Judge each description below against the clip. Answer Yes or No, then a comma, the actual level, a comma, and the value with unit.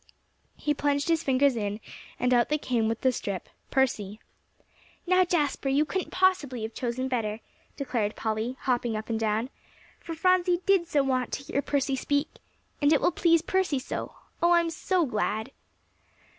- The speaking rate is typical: Yes, average, 170 wpm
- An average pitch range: No, wide, 6.0 semitones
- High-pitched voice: Yes, very high, 270 Hz